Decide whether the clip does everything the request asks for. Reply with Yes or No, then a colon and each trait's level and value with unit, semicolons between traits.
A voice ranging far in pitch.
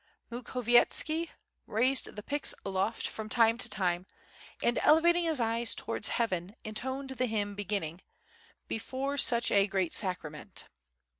No: average, 4.5 semitones